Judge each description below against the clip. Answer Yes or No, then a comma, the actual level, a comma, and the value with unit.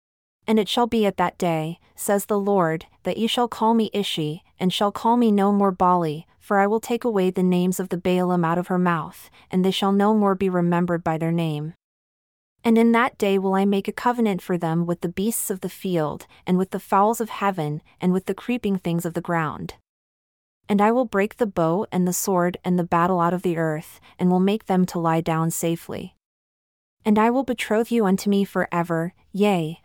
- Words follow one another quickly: Yes, fast, 225 wpm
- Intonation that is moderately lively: Yes, average, 3.3 semitones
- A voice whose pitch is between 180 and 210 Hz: Yes, high, 190 Hz